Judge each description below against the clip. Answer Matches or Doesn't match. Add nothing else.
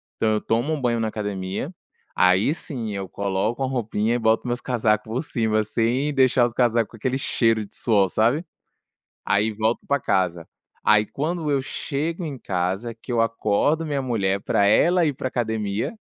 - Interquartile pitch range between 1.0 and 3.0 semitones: Doesn't match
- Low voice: Matches